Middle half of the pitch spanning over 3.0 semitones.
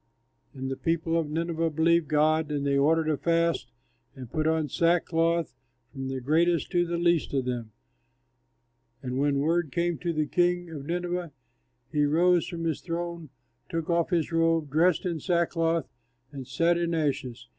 No: narrow, 2.6 semitones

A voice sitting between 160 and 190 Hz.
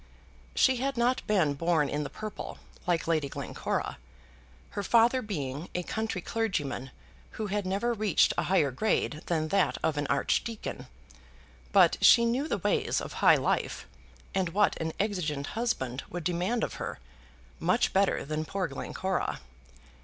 Yes: medium, 185 Hz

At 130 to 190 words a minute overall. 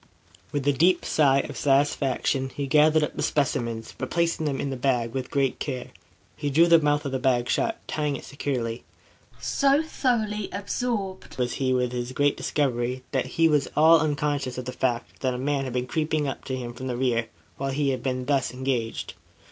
No: average, 200 wpm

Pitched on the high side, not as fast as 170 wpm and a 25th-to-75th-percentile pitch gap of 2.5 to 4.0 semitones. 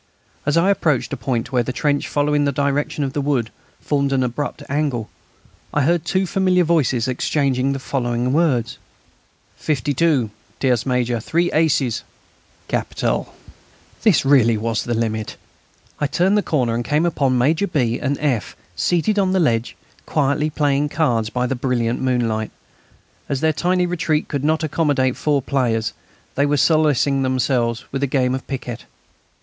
No: medium, 140 Hz; average, 160 wpm; average, 3.7 semitones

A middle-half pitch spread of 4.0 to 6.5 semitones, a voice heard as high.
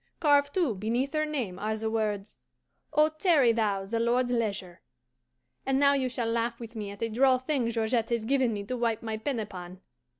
No: average, 3.5 semitones; high, 230 Hz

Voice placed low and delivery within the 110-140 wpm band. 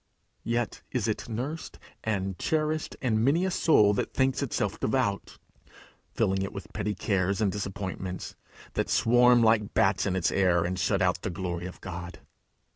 No: low, 100 Hz; average, 165 wpm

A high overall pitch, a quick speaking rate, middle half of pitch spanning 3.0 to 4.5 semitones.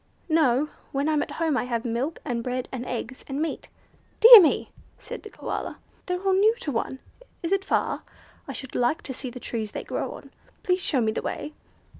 No: very high, 280 Hz; fast, 210 wpm; average, 5.2 semitones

